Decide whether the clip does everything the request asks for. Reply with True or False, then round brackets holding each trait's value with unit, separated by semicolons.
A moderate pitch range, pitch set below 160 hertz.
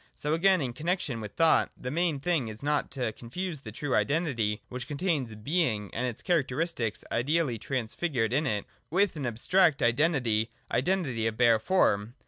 False (6.2 semitones; 135 Hz)